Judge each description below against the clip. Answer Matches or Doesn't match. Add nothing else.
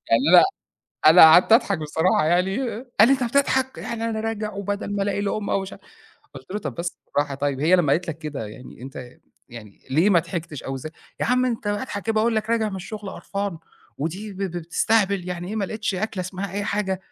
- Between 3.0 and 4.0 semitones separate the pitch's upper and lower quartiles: Doesn't match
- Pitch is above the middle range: Matches